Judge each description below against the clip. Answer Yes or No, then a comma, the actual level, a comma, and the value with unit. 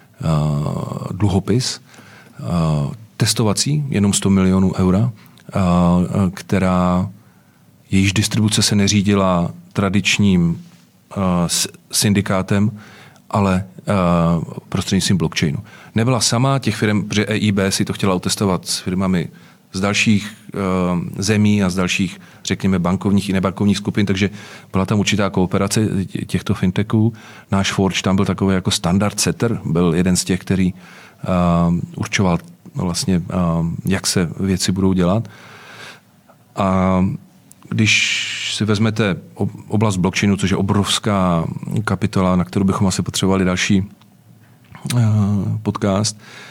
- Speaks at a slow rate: Yes, slow, 110 wpm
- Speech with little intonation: Yes, narrow, 2.0 semitones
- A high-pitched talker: No, low, 100 Hz